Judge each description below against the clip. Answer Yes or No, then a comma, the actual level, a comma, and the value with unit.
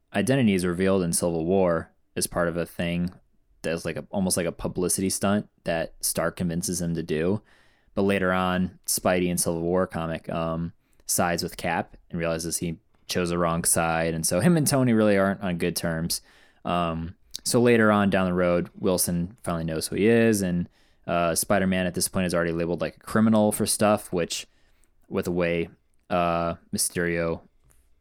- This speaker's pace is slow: No, average, 185 wpm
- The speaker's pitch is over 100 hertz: No, very low, 85 Hz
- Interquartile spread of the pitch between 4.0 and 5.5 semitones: No, narrow, 2.4 semitones